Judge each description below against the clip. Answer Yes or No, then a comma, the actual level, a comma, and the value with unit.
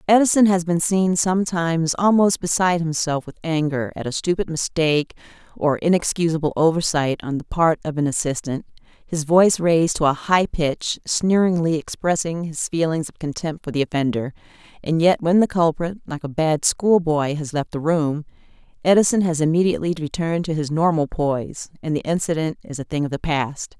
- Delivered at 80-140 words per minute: No, average, 175 wpm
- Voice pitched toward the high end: No, medium, 165 Hz